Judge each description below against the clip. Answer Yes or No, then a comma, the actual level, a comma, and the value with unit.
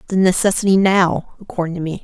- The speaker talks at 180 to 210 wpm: Yes, fast, 205 wpm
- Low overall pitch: No, medium, 185 Hz